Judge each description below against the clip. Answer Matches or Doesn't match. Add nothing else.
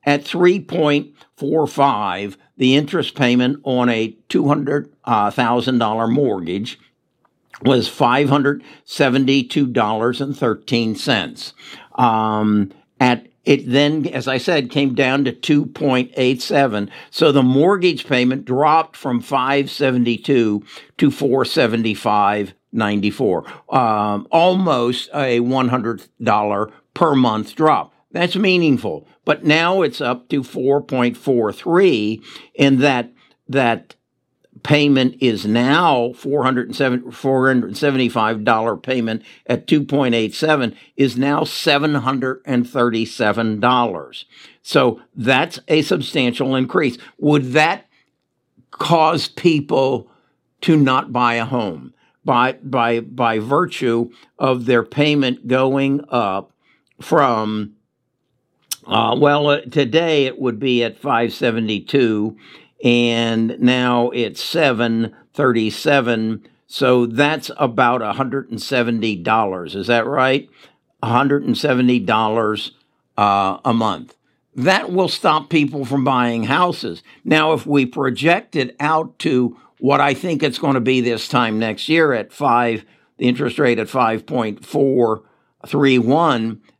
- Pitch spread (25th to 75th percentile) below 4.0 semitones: Matches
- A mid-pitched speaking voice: Doesn't match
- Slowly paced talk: Matches